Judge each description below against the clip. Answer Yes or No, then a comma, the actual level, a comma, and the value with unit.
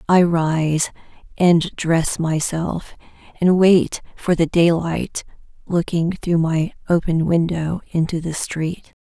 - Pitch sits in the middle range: Yes, medium, 165 Hz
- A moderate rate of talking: No, slow, 120 wpm